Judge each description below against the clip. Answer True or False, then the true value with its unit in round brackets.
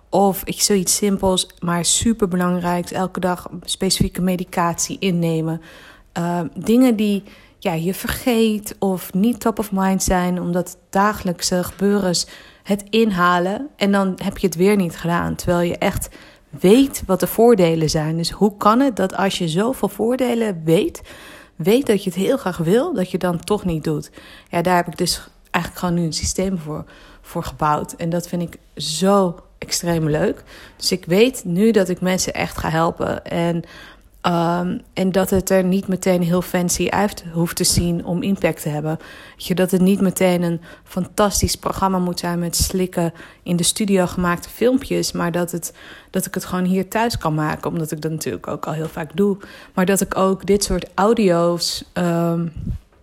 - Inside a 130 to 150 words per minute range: False (180 wpm)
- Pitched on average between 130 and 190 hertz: True (185 Hz)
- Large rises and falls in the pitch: False (2.5 semitones)